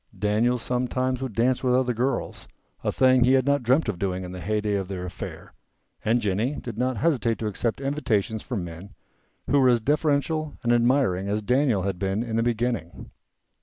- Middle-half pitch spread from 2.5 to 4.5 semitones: Yes, average, 4.0 semitones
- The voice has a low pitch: Yes, low, 120 Hz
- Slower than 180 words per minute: No, average, 195 wpm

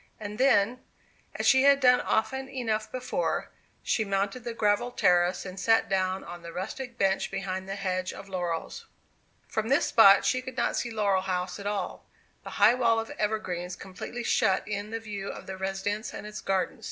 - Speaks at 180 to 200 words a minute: Yes, average, 190 wpm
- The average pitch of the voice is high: Yes, high, 205 Hz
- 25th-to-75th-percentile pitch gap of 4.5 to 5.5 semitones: No, average, 3.4 semitones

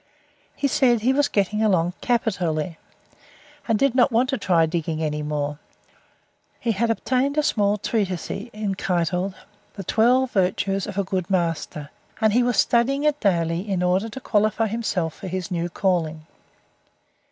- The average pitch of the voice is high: Yes, high, 195 Hz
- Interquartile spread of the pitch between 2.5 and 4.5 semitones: No, average, 5.2 semitones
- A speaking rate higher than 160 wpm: No, average, 155 wpm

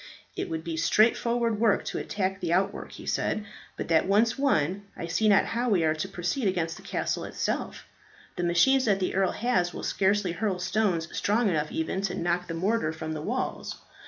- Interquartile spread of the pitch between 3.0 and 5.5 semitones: Yes, average, 4.2 semitones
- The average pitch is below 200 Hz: Yes, high, 190 Hz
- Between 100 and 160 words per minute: No, average, 200 wpm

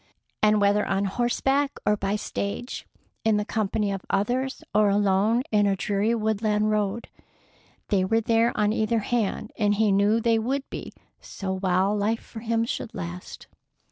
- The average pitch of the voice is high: Yes, high, 210 Hz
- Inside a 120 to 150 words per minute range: No, average, 165 wpm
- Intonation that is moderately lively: No, narrow, 2.1 semitones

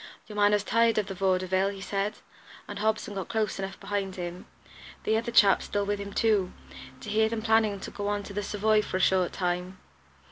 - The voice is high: Yes, high, 205 Hz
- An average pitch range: No, narrow, 1.9 semitones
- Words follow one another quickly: Yes, fast, 215 wpm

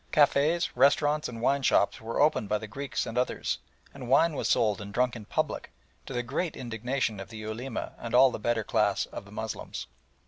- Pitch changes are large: No, average, 3.8 semitones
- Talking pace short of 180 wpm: No, fast, 205 wpm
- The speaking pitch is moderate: No, low, 125 Hz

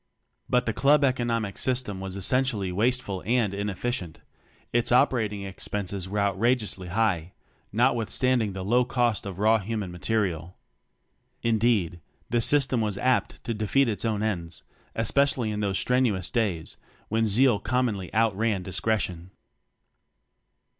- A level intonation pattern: No, average, 3.9 semitones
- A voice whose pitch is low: Yes, low, 110 Hz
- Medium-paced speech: No, slow, 130 wpm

